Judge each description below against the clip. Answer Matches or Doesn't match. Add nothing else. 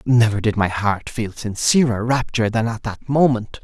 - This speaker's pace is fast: Doesn't match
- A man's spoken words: Matches